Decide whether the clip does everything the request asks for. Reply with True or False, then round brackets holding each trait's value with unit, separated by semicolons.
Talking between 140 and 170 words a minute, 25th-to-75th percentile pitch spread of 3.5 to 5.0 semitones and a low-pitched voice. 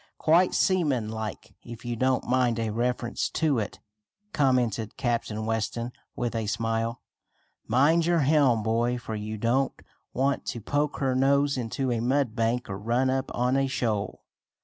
False (160 wpm; 3.1 semitones; 120 Hz)